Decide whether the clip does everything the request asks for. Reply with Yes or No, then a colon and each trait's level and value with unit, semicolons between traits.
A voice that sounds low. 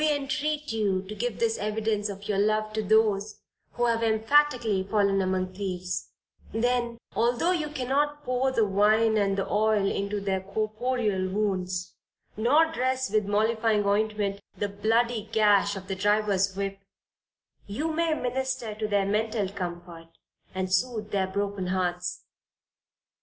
No: high, 210 Hz